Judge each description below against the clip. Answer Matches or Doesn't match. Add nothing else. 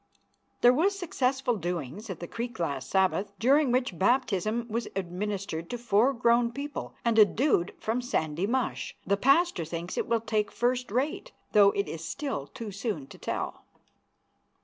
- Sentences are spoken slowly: Doesn't match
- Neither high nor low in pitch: Doesn't match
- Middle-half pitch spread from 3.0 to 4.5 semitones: Doesn't match